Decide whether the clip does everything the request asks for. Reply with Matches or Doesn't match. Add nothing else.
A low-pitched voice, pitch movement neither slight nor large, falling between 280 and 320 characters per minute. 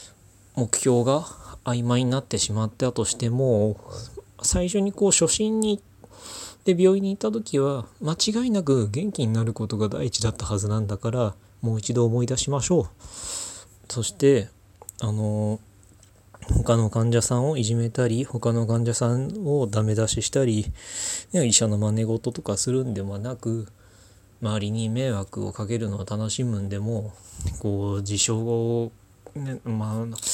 Matches